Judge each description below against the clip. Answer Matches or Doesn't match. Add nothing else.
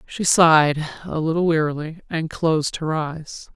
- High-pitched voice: Doesn't match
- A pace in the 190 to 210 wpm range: Doesn't match